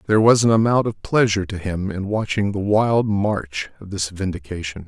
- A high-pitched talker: No, low, 100 Hz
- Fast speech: No, average, 195 wpm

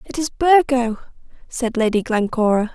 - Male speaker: No, female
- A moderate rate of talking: No, slow, 130 wpm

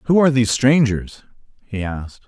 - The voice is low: Yes, low, 120 Hz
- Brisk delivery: No, average, 160 wpm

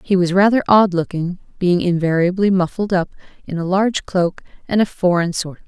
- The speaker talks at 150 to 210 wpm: Yes, average, 200 wpm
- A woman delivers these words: Yes, female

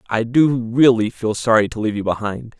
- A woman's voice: No, male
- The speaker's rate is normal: No, fast, 210 wpm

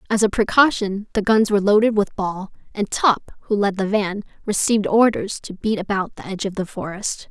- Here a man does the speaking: No, female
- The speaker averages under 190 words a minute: No, fast, 205 wpm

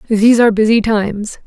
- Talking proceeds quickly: No, average, 165 wpm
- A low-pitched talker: No, high, 215 Hz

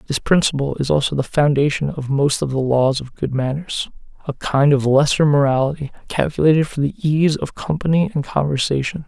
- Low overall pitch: No, medium, 145 Hz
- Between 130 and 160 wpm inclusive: No, average, 180 wpm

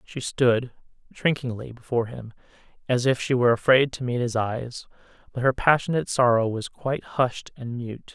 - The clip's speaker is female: No, male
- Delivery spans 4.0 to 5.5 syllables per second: Yes, 5.2 syllables/s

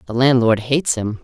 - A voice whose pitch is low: Yes, low, 125 Hz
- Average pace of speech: Yes, average, 195 wpm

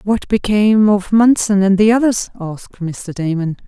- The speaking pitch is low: No, high, 205 Hz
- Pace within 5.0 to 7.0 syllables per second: No, 4.7 syllables/s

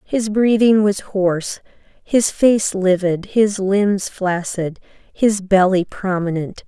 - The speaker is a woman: Yes, female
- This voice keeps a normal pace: No, slow, 115 wpm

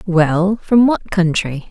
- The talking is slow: Yes, slow, 105 wpm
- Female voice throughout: Yes, female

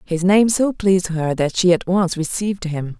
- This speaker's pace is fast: Yes, fast, 220 wpm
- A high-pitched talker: No, medium, 180 Hz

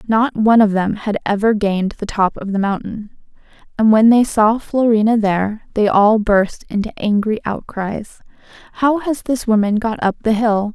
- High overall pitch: Yes, high, 215 Hz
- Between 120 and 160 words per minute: No, average, 180 wpm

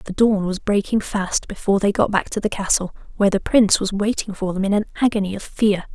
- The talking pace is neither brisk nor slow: No, fast, 240 wpm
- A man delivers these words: No, female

